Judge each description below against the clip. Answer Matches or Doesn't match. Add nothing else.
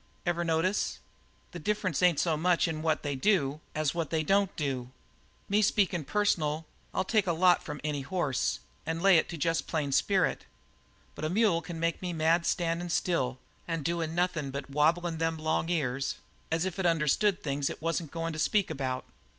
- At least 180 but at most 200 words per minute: Matches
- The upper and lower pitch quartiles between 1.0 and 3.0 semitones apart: Matches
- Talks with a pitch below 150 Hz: Doesn't match